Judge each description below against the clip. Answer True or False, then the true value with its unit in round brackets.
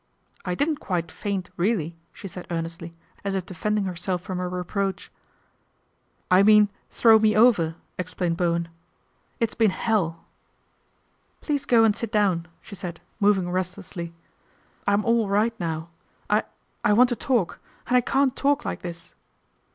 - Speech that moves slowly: False (160 wpm)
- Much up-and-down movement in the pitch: False (3.9 semitones)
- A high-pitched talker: True (195 Hz)